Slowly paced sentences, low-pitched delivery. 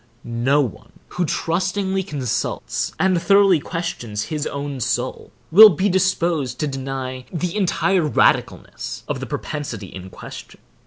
No: slow, 130 wpm; medium, 155 Hz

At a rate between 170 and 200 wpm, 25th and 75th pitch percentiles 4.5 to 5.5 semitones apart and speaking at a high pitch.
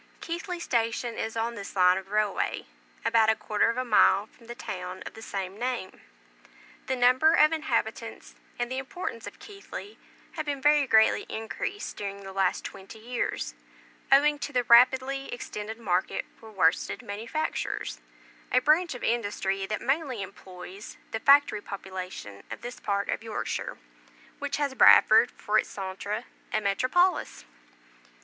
No: average, 155 wpm; average, 5.1 semitones; high, 230 Hz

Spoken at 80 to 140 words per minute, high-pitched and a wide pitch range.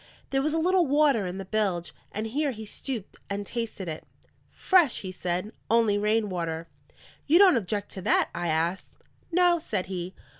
No: average, 180 wpm; high, 210 Hz; wide, 7.0 semitones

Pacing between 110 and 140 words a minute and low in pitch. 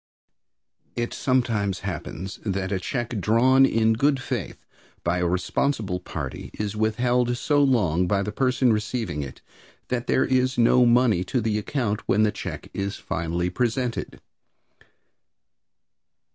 Yes: slow, 135 wpm; low, 110 Hz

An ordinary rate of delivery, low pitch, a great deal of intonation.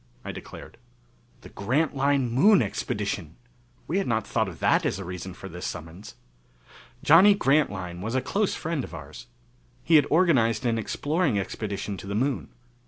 Yes: average, 165 wpm; low, 115 Hz; wide, 7.1 semitones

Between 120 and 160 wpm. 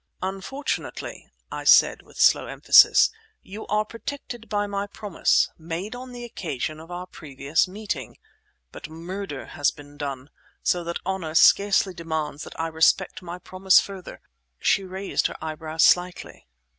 Yes: average, 145 wpm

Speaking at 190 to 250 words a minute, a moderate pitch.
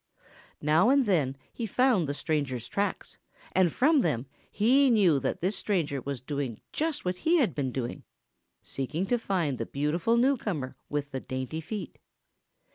No: average, 160 wpm; medium, 165 Hz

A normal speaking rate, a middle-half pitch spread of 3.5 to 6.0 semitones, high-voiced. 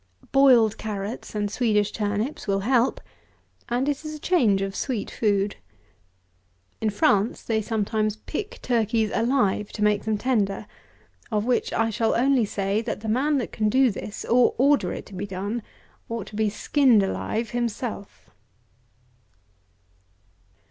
No: average, 150 wpm; average, 3.0 semitones; high, 220 Hz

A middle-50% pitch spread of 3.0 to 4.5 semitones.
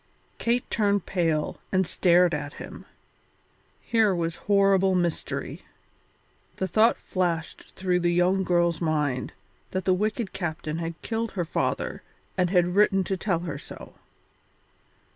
No: narrow, 2.6 semitones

